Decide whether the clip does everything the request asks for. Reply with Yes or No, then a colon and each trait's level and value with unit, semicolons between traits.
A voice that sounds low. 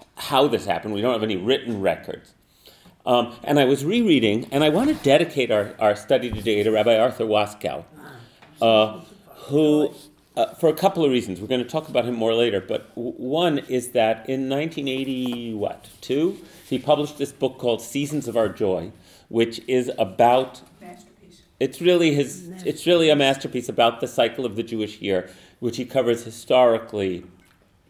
Yes: low, 125 Hz